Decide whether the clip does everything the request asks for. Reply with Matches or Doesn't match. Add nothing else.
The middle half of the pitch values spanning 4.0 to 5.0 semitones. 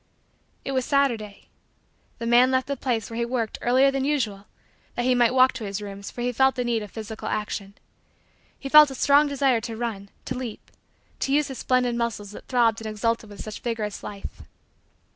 Doesn't match